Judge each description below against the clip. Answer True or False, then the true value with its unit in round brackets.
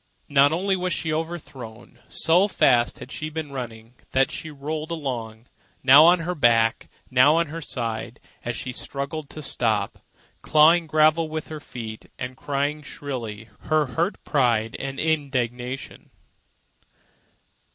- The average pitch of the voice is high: False (140 Hz)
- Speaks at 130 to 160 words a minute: True (140 wpm)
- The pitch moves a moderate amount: True (4.3 semitones)